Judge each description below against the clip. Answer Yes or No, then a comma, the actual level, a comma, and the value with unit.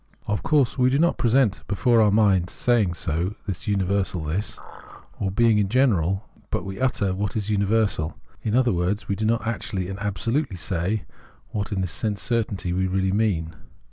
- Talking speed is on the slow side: No, average, 185 wpm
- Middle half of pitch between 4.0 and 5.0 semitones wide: No, average, 3.2 semitones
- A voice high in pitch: No, low, 100 Hz